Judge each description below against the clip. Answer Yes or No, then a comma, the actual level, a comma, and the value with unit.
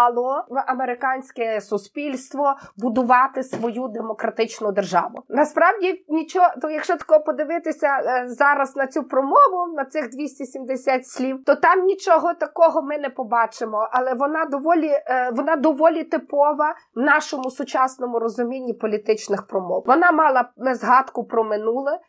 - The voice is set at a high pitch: Yes, very high, 270 Hz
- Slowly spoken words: No, average, 125 wpm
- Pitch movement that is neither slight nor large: Yes, average, 4.0 semitones